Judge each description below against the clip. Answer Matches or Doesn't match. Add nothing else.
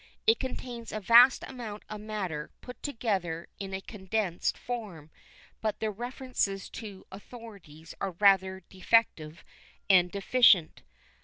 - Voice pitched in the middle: Doesn't match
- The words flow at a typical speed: Doesn't match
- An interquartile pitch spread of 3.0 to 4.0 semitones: Matches